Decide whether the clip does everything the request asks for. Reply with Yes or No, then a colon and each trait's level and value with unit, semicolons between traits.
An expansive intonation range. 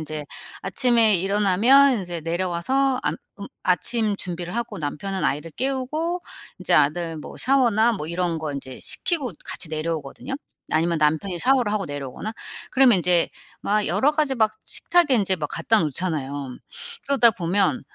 Yes: wide, 7.2 semitones